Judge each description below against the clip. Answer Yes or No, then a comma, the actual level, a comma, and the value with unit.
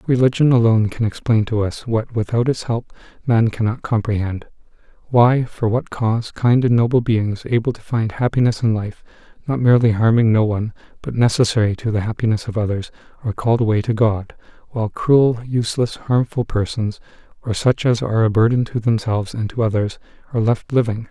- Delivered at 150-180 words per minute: Yes, average, 175 wpm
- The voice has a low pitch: Yes, low, 115 Hz